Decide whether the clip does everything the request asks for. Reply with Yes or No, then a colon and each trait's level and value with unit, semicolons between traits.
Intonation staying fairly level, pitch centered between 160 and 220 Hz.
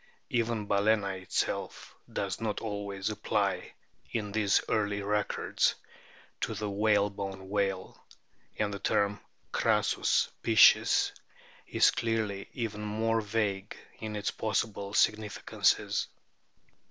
No: narrow, 1.5 semitones; low, 105 Hz